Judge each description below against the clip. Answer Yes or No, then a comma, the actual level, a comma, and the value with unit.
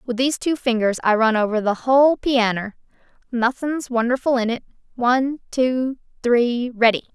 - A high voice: Yes, high, 245 Hz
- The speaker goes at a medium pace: Yes, average, 145 wpm